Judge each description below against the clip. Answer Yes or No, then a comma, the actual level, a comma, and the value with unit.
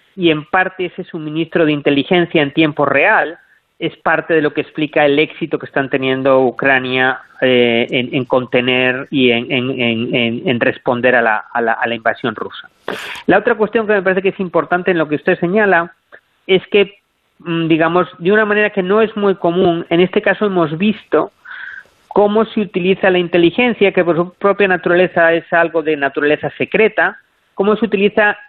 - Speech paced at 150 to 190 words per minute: Yes, average, 185 wpm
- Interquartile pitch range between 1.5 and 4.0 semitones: No, average, 4.8 semitones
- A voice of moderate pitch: Yes, medium, 170 Hz